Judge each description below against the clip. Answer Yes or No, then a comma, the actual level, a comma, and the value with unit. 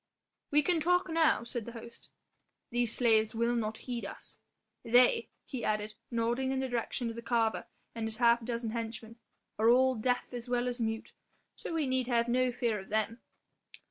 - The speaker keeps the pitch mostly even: Yes, narrow, 1.9 semitones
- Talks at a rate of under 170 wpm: No, average, 185 wpm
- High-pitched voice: Yes, high, 235 Hz